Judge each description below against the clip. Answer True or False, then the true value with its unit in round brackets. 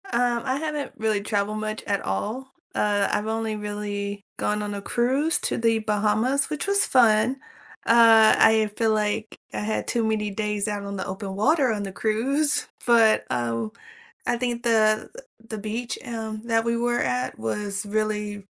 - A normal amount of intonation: False (2.3 semitones)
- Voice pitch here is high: True (215 Hz)